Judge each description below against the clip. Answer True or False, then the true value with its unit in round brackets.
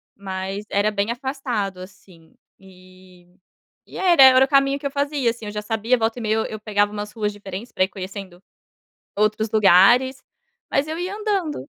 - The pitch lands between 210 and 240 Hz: True (215 Hz)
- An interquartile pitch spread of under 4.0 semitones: False (5.2 semitones)